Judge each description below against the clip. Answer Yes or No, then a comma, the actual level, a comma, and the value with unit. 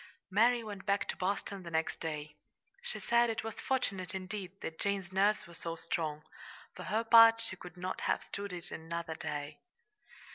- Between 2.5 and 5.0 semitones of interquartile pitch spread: Yes, average, 4.2 semitones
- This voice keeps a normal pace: Yes, average, 180 wpm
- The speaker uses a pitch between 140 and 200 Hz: Yes, high, 190 Hz